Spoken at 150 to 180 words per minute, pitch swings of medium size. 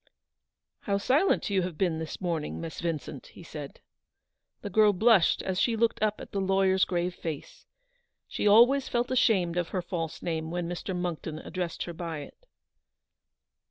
Yes: average, 170 wpm; average, 3.8 semitones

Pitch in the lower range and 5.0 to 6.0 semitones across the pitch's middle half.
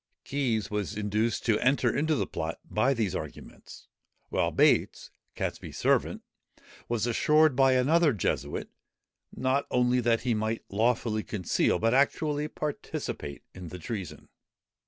No: low, 115 Hz; average, 4.2 semitones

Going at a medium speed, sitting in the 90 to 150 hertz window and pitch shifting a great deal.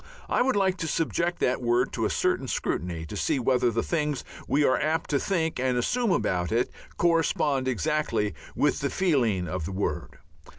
Yes: average, 185 wpm; low, 135 Hz; wide, 6.0 semitones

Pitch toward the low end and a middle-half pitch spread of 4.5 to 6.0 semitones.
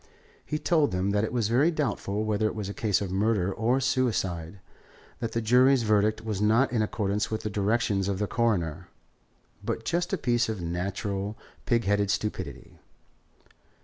No: low, 110 Hz; average, 3.0 semitones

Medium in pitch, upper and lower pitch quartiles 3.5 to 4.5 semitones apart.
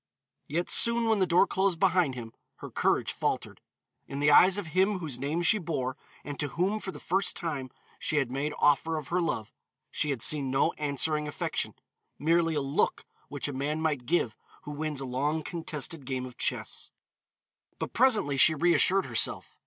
Yes: medium, 155 Hz; average, 4.0 semitones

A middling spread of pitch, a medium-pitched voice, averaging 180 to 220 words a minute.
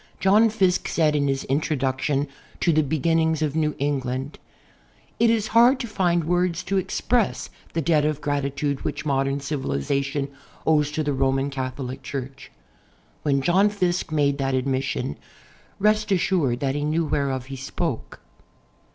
No: average, 4.0 semitones; medium, 145 Hz; average, 150 wpm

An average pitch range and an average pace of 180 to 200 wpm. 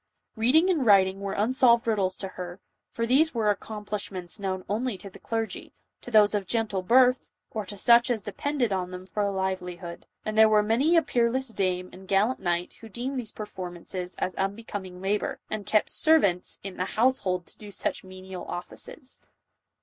Yes: average, 3.9 semitones; average, 185 wpm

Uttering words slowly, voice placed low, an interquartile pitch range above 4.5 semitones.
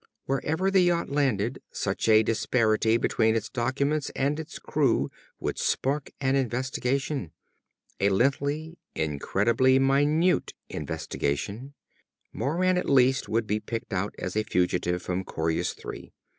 Yes: slow, 130 wpm; low, 125 Hz; wide, 5.4 semitones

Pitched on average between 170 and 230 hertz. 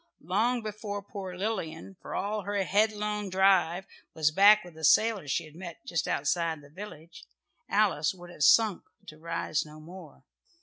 Yes: medium, 185 Hz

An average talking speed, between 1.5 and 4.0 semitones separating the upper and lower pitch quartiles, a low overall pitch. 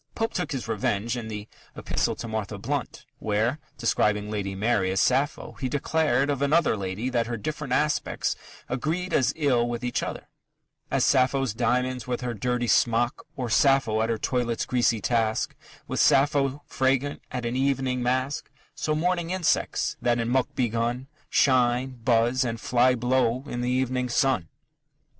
Yes: average, 160 wpm; average, 2.7 semitones; low, 125 Hz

